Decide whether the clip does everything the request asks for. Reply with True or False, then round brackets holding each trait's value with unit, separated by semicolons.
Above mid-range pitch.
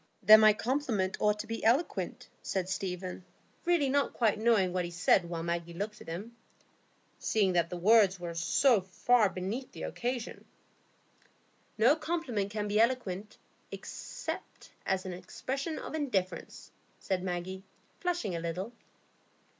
True (205 Hz)